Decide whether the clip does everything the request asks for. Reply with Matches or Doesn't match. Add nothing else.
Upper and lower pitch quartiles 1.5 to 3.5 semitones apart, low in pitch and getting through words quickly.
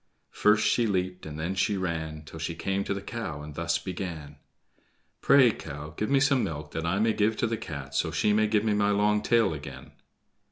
Doesn't match